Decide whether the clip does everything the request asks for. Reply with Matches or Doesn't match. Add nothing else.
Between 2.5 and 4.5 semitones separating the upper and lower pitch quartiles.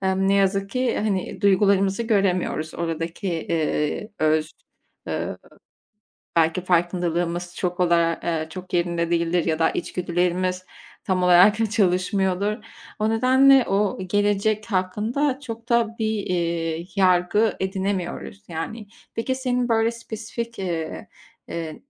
Matches